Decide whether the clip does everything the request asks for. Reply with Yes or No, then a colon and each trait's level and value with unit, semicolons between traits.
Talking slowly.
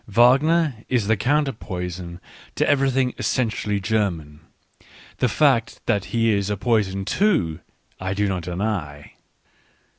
Yes: slow, 130 wpm